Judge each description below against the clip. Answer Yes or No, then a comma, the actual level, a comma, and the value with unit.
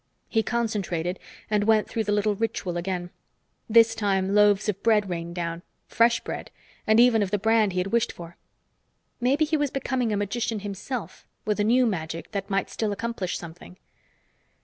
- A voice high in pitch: Yes, high, 210 Hz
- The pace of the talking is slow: No, average, 175 wpm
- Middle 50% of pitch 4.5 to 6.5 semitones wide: No, average, 3.4 semitones